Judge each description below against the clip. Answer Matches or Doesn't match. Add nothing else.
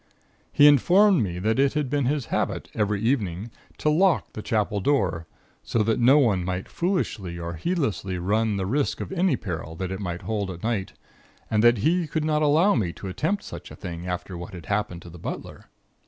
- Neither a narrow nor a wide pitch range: Doesn't match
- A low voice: Matches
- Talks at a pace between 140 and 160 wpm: Doesn't match